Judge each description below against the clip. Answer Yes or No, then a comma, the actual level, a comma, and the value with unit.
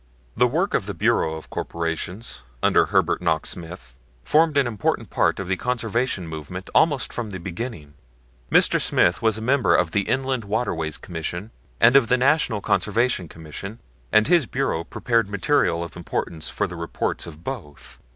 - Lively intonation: Yes, wide, 6.7 semitones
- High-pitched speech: No, low, 100 Hz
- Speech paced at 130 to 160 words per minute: No, average, 170 wpm